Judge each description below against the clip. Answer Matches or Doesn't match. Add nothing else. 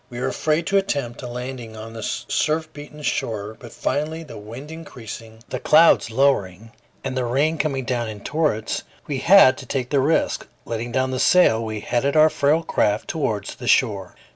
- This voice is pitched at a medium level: Doesn't match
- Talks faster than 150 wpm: Matches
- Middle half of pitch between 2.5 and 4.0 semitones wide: Doesn't match